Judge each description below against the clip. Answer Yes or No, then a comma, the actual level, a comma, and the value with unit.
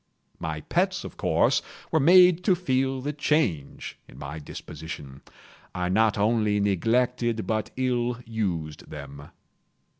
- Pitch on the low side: Yes, low, 110 Hz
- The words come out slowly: Yes, slow, 125 wpm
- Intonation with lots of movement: Yes, wide, 8.0 semitones